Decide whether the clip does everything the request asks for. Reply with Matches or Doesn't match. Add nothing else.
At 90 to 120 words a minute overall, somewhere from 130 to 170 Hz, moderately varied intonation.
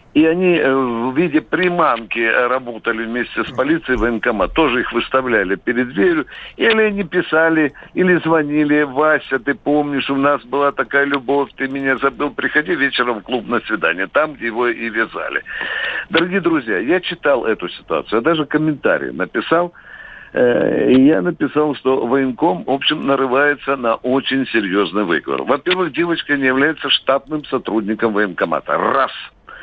Doesn't match